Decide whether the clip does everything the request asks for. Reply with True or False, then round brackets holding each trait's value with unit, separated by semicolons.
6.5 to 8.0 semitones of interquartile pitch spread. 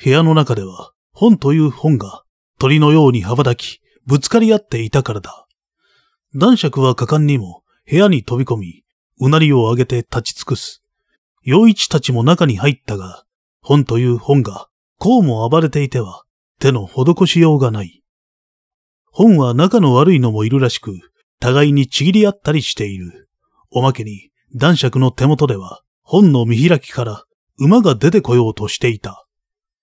False (5.1 semitones)